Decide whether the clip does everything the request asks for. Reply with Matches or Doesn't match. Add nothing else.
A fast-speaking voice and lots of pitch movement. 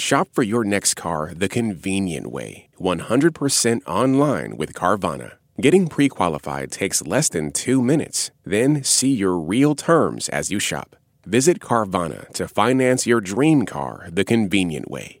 Doesn't match